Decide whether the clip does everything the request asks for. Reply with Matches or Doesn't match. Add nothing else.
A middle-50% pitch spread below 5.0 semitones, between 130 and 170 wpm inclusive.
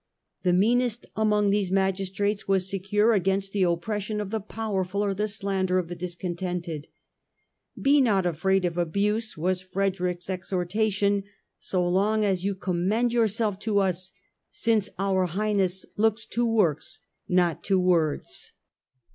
Matches